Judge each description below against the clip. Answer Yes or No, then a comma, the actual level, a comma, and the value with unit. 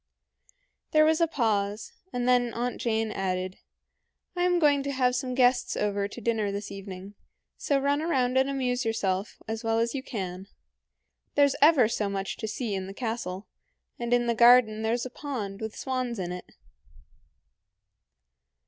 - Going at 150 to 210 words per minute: Yes, average, 165 wpm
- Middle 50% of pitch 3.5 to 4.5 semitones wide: Yes, average, 4.1 semitones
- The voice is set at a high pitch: Yes, high, 235 Hz